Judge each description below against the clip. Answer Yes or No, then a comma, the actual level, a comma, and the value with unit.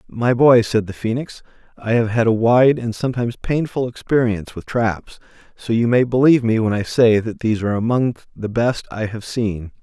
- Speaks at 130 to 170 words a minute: No, average, 200 wpm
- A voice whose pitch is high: No, low, 115 Hz